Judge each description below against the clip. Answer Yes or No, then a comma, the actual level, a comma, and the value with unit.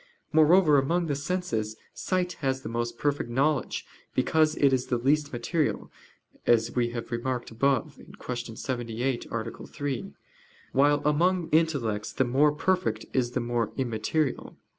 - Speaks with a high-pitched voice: No, low, 135 Hz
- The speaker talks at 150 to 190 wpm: No, average, 140 wpm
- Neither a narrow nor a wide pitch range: Yes, average, 4.4 semitones